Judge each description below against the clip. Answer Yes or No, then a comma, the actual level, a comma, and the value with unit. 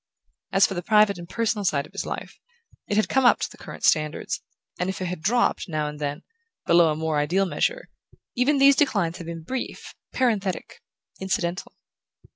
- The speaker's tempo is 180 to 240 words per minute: Yes, average, 190 wpm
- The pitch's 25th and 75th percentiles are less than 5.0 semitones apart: No, average, 5.3 semitones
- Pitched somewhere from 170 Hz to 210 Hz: Yes, high, 190 Hz